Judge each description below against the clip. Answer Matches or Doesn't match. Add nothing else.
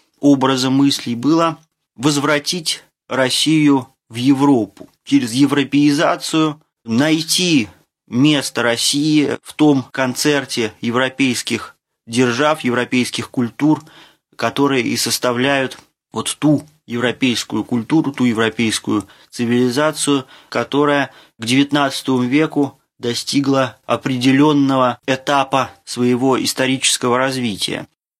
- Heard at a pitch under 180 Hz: Matches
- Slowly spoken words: Matches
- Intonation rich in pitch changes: Doesn't match